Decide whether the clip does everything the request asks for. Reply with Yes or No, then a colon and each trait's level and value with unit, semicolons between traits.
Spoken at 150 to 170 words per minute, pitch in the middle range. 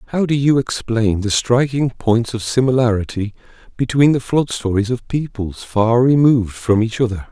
No: average, 165 wpm; low, 120 Hz